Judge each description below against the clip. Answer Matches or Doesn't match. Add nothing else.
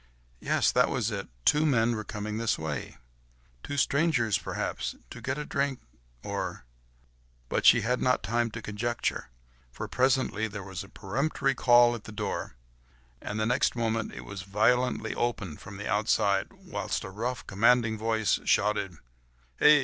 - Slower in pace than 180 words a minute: Matches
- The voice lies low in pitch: Matches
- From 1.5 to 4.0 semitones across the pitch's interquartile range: Matches